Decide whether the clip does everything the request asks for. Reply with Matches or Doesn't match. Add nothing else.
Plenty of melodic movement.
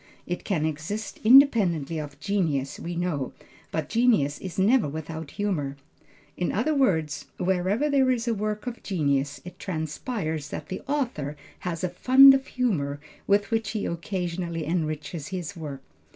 Matches